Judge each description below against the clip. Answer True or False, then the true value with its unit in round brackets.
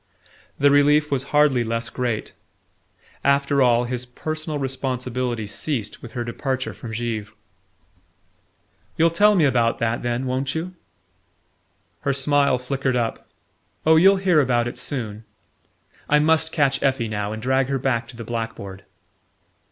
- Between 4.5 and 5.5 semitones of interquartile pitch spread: False (3.5 semitones)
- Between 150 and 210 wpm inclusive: False (140 wpm)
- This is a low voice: True (130 Hz)